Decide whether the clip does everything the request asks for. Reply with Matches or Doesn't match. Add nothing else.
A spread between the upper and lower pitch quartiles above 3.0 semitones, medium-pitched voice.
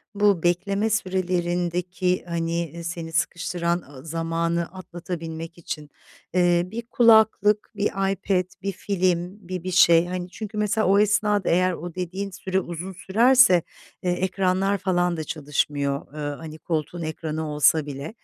Doesn't match